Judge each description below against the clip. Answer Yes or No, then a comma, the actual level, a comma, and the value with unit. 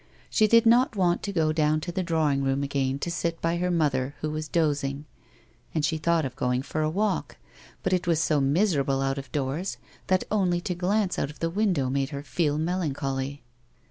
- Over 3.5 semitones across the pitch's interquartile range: Yes, average, 4.2 semitones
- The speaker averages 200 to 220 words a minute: Yes, fast, 205 wpm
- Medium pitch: Yes, medium, 155 Hz